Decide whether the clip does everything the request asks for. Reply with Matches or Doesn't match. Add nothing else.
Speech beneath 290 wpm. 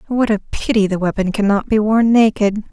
Matches